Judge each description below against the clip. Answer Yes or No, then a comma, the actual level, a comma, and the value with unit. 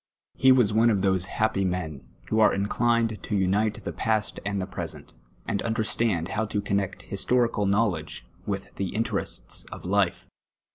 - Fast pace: No, average, 160 wpm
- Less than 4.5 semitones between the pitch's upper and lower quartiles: Yes, narrow, 2.4 semitones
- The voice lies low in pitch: Yes, low, 100 Hz